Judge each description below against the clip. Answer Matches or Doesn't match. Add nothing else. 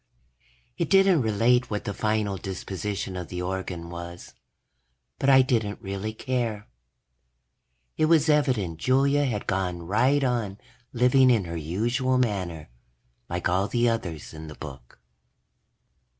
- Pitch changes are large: Matches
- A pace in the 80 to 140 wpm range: Matches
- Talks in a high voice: Doesn't match